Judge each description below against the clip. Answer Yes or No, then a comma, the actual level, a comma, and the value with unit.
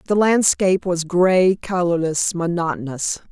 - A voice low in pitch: No, medium, 180 Hz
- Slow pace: Yes, slow, 110 wpm